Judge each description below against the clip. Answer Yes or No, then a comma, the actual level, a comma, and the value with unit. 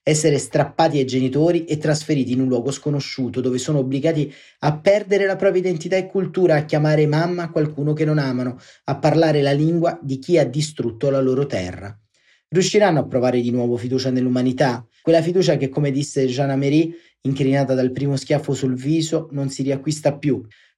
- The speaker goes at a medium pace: No, fast, 175 wpm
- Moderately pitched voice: Yes, medium, 145 Hz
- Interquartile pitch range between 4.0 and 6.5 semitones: No, average, 3.4 semitones